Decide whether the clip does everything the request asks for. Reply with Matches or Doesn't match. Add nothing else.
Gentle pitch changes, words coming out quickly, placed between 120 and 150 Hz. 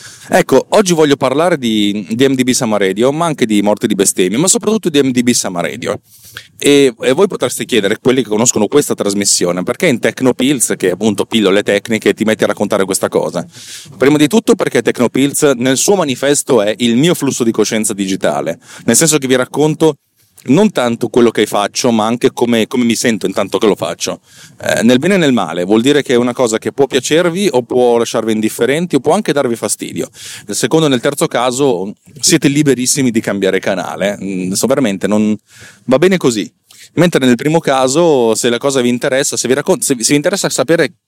Doesn't match